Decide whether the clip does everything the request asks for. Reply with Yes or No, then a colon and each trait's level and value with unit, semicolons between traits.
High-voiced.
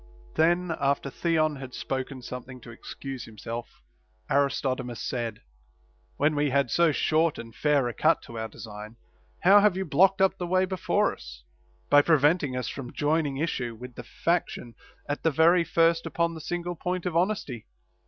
No: medium, 145 Hz